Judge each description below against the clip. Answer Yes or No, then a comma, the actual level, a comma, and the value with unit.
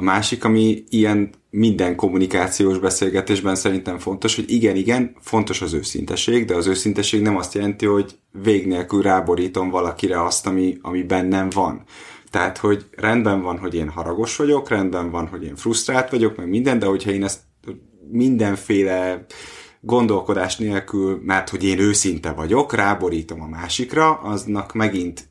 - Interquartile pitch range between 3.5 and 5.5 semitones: No, average, 2.7 semitones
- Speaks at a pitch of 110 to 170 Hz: No, very low, 95 Hz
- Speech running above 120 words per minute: Yes, average, 150 wpm